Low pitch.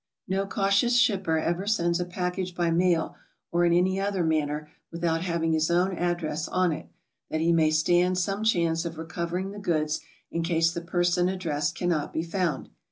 No: medium, 175 Hz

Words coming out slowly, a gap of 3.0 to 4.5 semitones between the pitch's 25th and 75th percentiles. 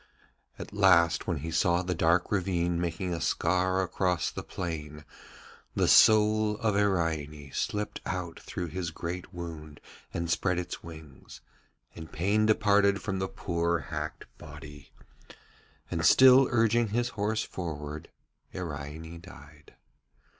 Yes: slow, 130 wpm; average, 3.8 semitones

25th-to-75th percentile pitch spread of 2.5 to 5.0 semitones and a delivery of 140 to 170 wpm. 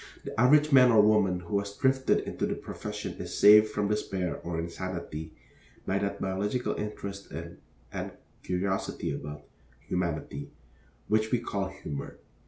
Yes: average, 3.8 semitones; average, 145 wpm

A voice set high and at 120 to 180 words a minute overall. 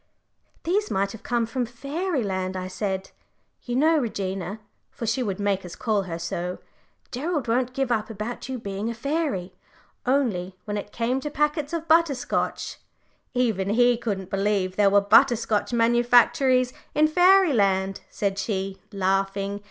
Yes: high, 225 Hz; average, 160 wpm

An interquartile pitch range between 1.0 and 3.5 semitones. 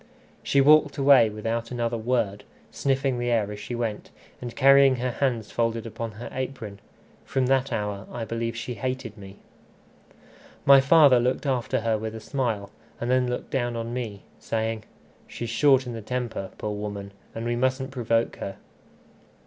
Yes: average, 2.8 semitones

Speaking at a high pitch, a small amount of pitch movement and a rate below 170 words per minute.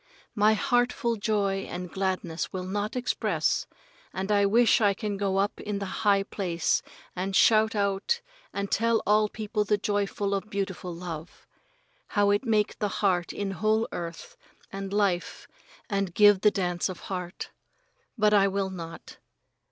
Yes: high, 200 Hz; narrow, 1.9 semitones; average, 150 wpm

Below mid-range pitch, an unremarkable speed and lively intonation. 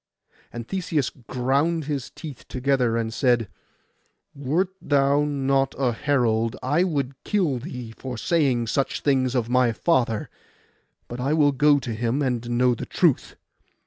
No: low, 130 Hz; average, 145 wpm; average, 3.2 semitones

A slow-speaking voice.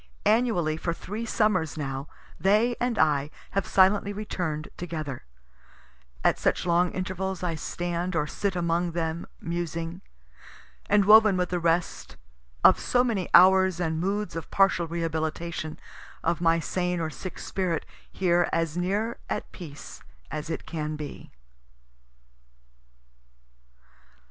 Yes: slow, 130 wpm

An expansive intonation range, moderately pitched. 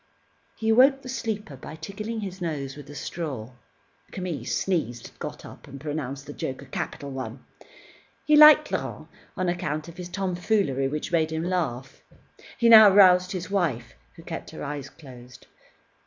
Yes: wide, 6.1 semitones; medium, 165 Hz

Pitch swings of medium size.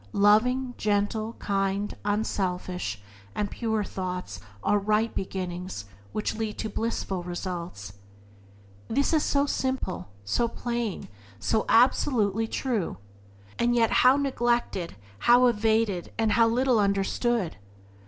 Yes: average, 3.8 semitones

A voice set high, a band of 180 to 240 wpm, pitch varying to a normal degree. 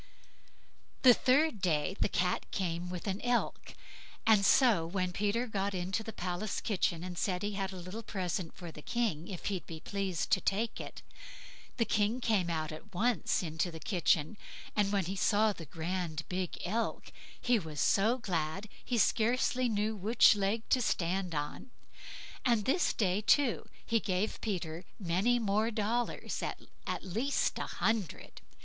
No: high, 195 Hz; average, 165 wpm; average, 3.9 semitones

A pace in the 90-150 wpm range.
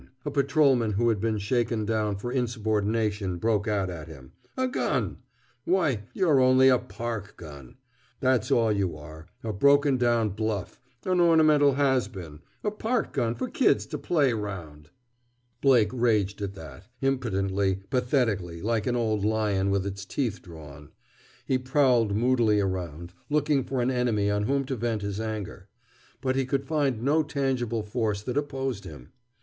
No: average, 160 wpm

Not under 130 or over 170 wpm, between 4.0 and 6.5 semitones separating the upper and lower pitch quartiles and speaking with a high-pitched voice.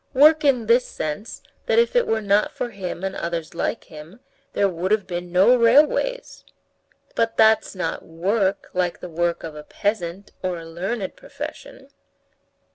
Yes: average, 165 wpm; average, 5.2 semitones; high, 195 Hz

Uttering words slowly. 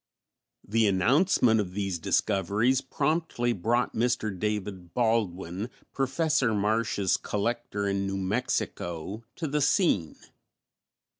Yes: slow, 100 wpm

